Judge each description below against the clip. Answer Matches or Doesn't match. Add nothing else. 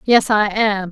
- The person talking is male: Doesn't match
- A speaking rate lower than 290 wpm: Matches